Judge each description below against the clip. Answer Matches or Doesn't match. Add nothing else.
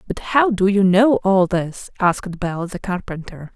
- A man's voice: Doesn't match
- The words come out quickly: Doesn't match